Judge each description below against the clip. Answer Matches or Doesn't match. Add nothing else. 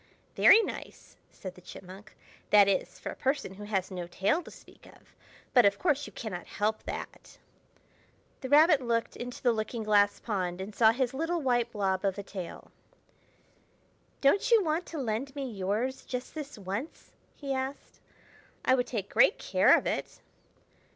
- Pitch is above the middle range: Matches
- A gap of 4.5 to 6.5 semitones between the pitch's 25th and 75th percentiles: Matches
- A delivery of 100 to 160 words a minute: Doesn't match